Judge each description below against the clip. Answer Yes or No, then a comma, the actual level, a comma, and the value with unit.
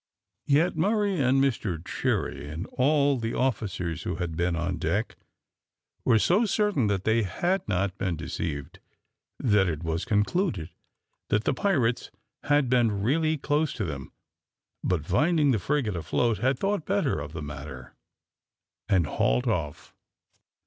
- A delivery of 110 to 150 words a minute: Yes, average, 145 wpm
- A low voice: Yes, low, 110 Hz